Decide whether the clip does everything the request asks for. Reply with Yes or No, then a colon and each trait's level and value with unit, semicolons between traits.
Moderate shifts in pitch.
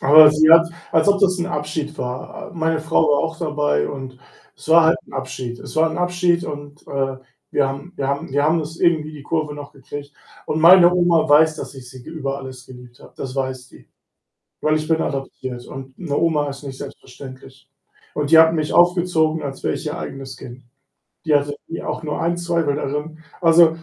Yes: average, 3.1 semitones